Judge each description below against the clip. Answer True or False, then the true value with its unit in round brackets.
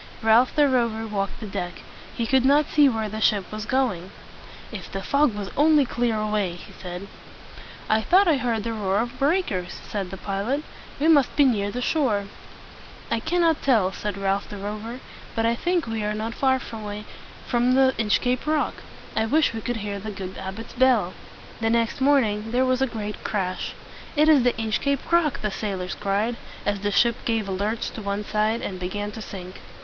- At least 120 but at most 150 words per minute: False (195 wpm)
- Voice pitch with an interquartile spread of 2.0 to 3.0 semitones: False (4.1 semitones)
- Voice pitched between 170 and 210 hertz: False (225 Hz)